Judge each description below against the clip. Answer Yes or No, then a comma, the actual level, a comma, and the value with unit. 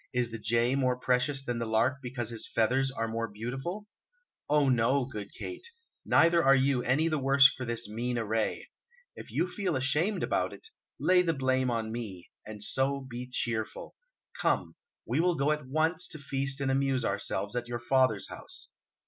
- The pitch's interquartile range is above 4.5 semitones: No, average, 3.0 semitones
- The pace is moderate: Yes, average, 180 wpm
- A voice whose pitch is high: No, low, 130 Hz